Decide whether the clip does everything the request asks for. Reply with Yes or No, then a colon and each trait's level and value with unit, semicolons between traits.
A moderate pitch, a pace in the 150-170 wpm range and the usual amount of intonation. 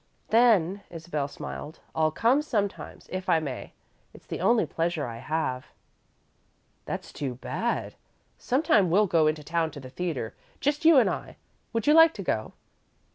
No: medium, 170 Hz; average, 160 wpm; wide, 7.1 semitones